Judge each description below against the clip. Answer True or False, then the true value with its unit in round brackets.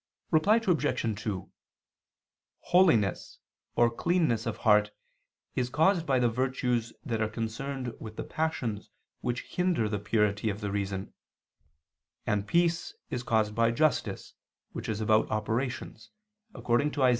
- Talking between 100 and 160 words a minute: True (135 wpm)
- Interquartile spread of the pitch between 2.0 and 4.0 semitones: False (4.6 semitones)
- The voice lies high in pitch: False (115 Hz)